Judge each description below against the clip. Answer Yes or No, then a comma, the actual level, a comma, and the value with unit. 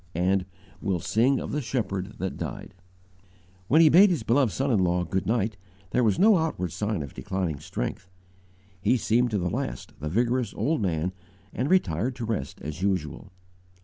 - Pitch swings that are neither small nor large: No, wide, 5.7 semitones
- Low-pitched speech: Yes, low, 105 Hz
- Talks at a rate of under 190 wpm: Yes, average, 180 wpm